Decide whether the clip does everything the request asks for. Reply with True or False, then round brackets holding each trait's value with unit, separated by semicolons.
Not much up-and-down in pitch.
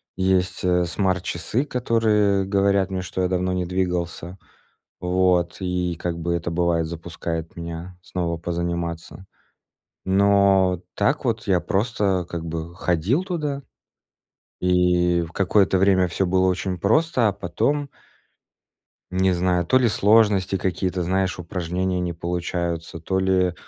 True (2.1 semitones)